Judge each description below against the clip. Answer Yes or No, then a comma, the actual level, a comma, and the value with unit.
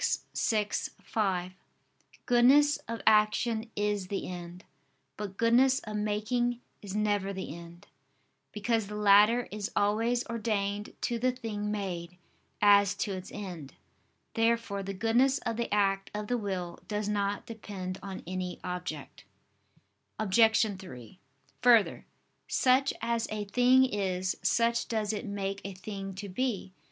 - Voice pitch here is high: Yes, high, 210 Hz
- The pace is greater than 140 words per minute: No, slow, 135 wpm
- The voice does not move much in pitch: No, average, 3.0 semitones